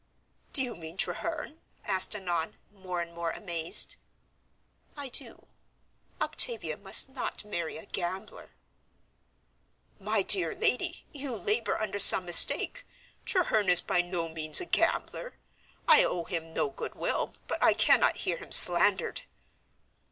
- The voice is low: No, high, 190 Hz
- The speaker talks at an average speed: No, slow, 130 wpm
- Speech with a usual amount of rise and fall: Yes, average, 4.9 semitones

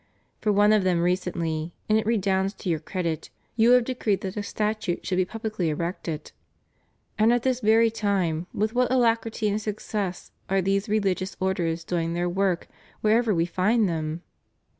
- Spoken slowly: No, average, 175 wpm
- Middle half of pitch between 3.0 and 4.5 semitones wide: Yes, average, 3.8 semitones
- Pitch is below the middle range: No, high, 195 Hz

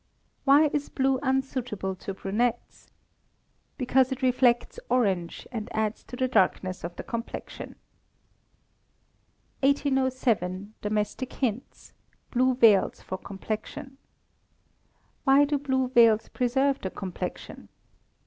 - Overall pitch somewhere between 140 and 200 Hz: No, very high, 250 Hz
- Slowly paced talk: Yes, slow, 105 wpm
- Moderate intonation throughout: Yes, average, 4.1 semitones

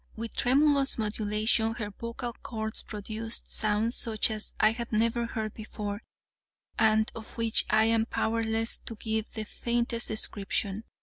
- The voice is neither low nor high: No, high, 220 Hz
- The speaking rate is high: No, average, 140 wpm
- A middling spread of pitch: No, narrow, 1.2 semitones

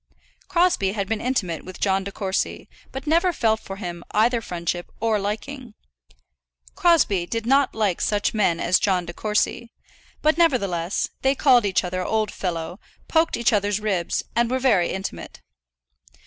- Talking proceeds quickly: No, average, 160 wpm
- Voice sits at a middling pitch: No, high, 210 Hz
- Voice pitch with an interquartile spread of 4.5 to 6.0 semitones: Yes, average, 5.0 semitones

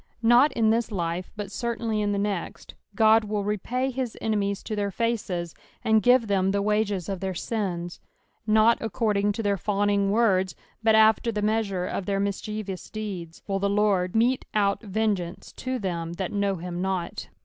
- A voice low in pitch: No, high, 205 Hz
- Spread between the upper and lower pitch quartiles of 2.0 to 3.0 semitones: Yes, narrow, 2.4 semitones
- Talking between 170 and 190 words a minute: Yes, average, 175 wpm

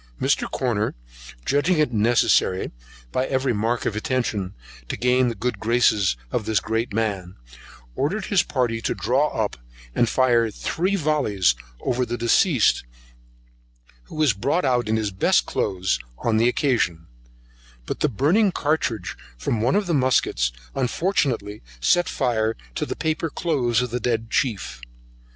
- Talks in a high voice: No, low, 120 Hz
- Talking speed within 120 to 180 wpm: Yes, average, 150 wpm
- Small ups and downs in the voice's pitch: No, average, 4.5 semitones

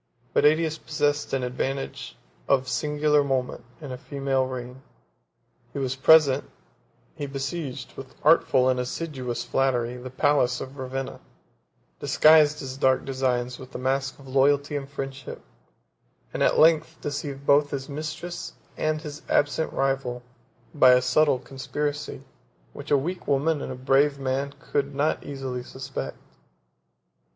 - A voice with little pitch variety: Yes, narrow, 2.1 semitones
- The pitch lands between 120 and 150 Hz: Yes, low, 135 Hz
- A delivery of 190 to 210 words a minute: No, average, 140 wpm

